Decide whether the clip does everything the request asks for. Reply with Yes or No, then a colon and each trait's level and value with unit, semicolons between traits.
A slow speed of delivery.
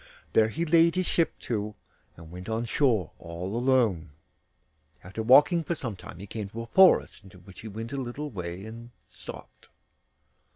No: average, 175 wpm